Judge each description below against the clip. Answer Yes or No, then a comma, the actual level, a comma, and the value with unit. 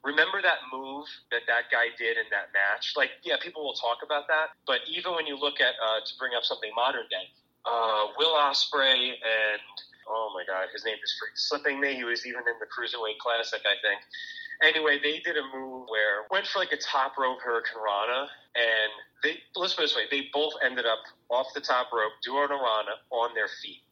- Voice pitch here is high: No, low, 135 Hz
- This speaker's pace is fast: Yes, fast, 215 wpm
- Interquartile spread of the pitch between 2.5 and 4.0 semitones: No, average, 4.7 semitones